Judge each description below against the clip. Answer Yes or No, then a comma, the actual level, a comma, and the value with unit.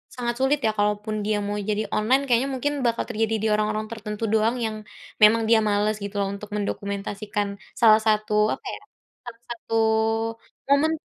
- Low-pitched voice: No, high, 215 Hz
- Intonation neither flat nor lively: No, narrow, 2.1 semitones